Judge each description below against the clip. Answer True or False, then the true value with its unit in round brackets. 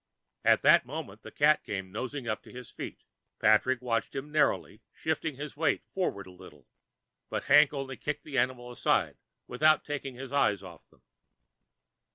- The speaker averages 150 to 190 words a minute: True (170 wpm)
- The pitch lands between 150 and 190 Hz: False (130 Hz)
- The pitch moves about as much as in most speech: True (5.0 semitones)